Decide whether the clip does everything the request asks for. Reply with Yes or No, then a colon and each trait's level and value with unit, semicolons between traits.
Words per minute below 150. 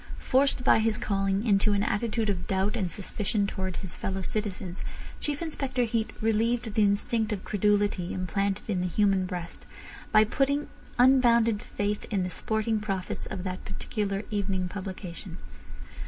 No: average, 155 wpm